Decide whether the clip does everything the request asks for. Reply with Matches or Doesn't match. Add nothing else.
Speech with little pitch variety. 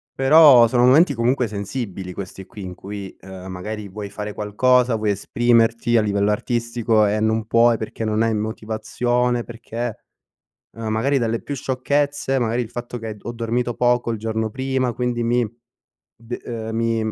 Matches